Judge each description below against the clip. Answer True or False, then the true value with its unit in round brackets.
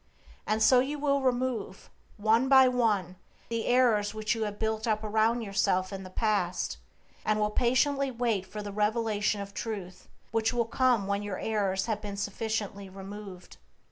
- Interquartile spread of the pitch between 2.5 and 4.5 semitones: True (2.8 semitones)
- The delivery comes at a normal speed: True (165 wpm)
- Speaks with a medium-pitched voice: False (215 Hz)